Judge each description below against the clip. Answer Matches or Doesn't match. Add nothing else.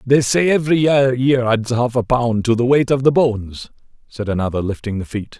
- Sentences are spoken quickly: Matches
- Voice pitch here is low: Matches